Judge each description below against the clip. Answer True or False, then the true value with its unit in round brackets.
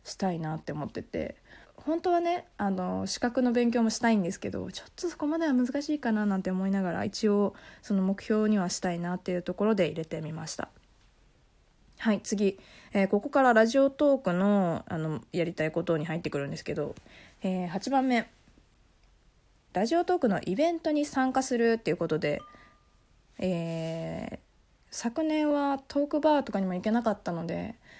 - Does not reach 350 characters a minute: False (355 characters per minute)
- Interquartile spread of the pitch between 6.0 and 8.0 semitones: True (7.0 semitones)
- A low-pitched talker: False (205 Hz)